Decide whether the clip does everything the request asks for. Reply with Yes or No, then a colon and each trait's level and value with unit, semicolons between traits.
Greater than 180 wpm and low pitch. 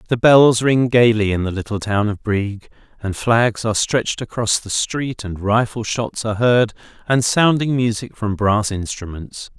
No: average, 175 wpm; low, 110 Hz